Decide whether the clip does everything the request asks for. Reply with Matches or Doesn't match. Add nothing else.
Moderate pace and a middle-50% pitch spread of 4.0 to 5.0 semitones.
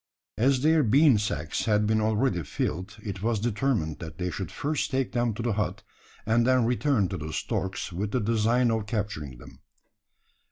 Matches